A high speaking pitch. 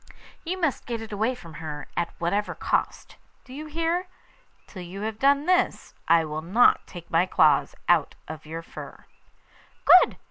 Yes: high, 200 Hz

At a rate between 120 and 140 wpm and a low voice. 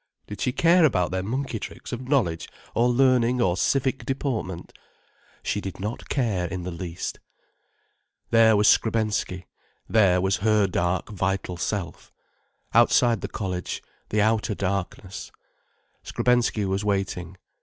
Yes: slow, 135 wpm; low, 105 Hz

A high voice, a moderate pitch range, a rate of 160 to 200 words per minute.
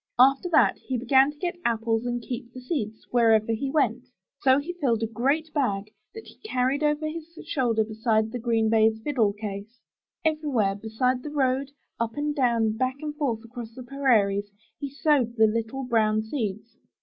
Yes: high, 245 Hz; average, 4.0 semitones; average, 180 wpm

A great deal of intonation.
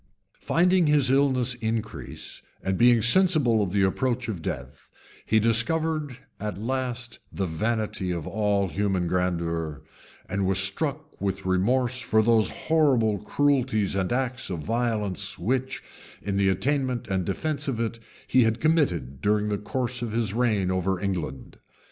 No: average, 5.0 semitones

